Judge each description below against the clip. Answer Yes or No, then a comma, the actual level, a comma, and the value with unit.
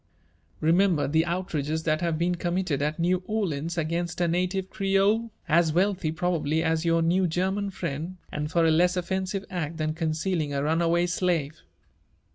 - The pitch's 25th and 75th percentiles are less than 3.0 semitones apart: Yes, narrow, 2.5 semitones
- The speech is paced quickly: No, average, 165 wpm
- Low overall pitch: No, medium, 170 Hz